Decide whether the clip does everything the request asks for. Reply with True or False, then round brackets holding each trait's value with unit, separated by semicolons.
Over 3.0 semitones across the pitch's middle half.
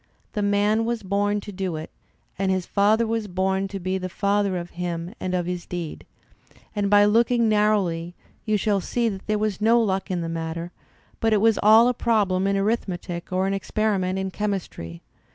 False (2.6 semitones)